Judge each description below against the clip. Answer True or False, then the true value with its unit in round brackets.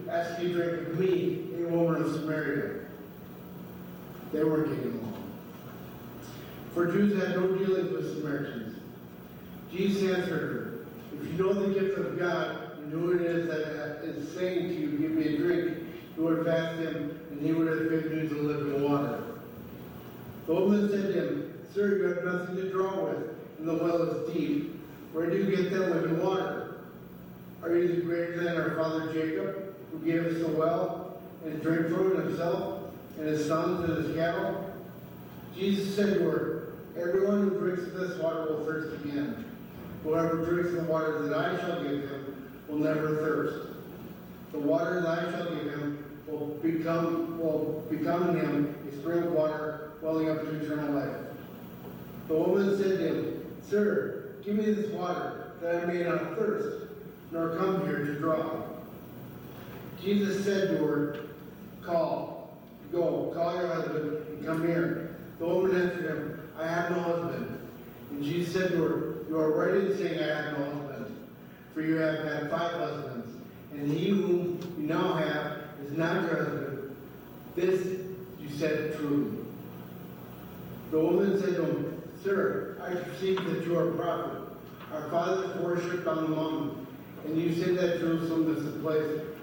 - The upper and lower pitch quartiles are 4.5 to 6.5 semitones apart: False (2.6 semitones)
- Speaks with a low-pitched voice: False (160 Hz)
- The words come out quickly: False (170 wpm)